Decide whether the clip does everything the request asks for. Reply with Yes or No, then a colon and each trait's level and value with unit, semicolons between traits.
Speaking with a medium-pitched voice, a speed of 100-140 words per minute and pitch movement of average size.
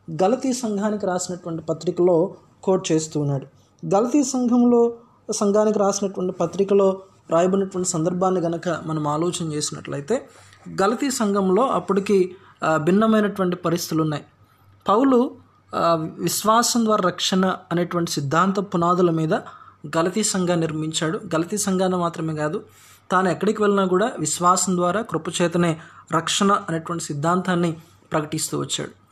Yes: medium, 180 Hz; average, 105 wpm; average, 3.6 semitones